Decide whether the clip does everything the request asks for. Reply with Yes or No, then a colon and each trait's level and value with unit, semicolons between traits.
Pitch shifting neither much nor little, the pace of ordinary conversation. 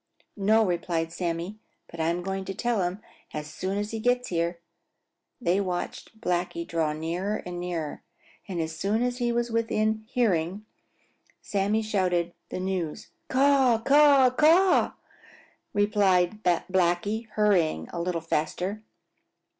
No: average, 4.3 semitones; slow, 130 wpm